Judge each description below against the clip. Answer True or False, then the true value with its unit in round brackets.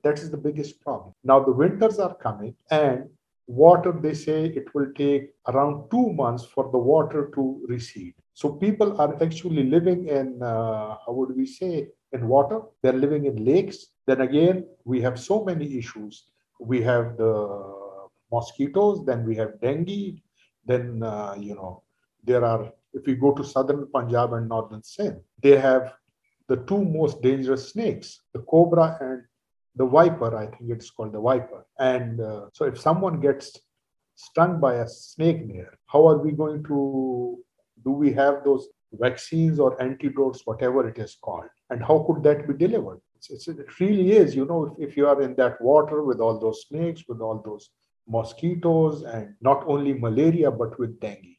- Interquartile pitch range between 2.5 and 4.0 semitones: False (4.5 semitones)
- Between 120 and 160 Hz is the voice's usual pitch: True (135 Hz)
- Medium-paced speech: True (175 wpm)